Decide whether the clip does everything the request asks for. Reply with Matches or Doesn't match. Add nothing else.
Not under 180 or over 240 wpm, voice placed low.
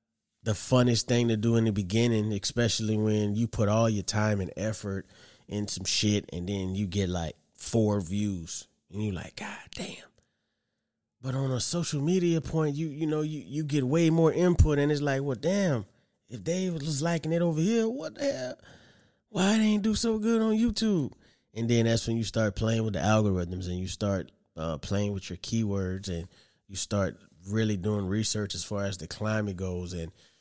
Matches